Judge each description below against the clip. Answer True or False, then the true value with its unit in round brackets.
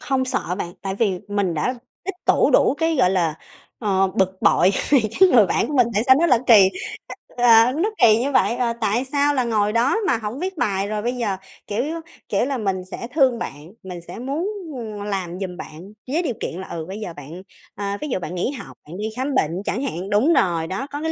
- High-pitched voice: True (215 Hz)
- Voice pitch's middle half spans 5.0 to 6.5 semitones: True (5.5 semitones)